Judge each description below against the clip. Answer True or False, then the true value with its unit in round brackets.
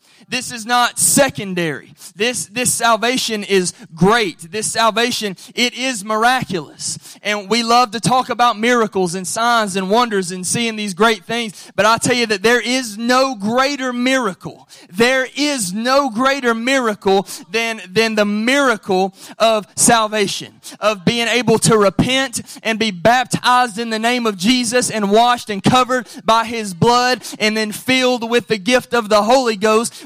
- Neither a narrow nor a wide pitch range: True (3.0 semitones)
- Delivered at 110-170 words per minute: True (160 wpm)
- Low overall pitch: False (230 Hz)